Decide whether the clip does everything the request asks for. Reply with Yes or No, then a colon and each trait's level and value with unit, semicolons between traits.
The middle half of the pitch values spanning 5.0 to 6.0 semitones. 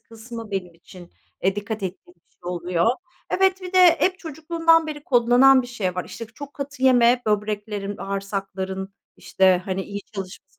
Yes: wide, 5.6 semitones